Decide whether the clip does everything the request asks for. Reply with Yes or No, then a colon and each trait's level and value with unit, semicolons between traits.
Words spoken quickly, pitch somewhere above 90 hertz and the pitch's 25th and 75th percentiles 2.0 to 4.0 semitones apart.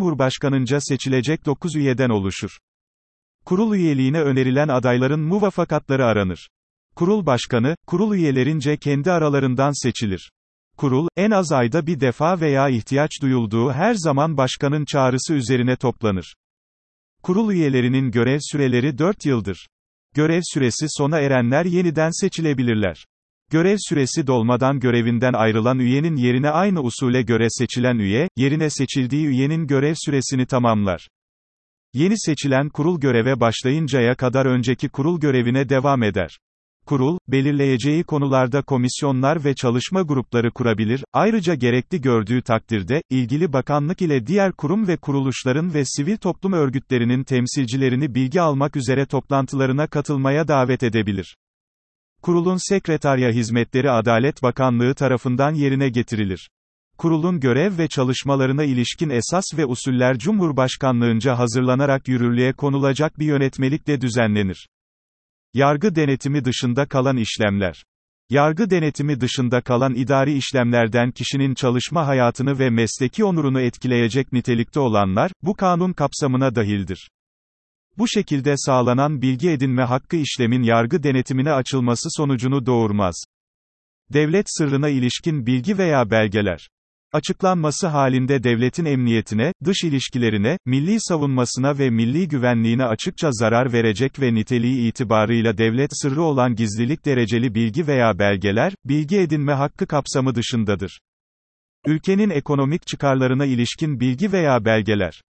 No: average, 120 wpm; low, 135 Hz; average, 3.7 semitones